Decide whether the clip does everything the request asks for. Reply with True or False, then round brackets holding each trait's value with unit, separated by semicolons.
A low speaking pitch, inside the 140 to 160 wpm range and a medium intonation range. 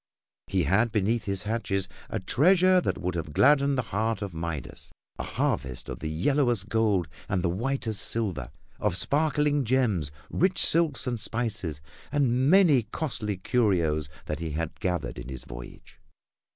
False (105 Hz; 150 wpm; 7.4 semitones)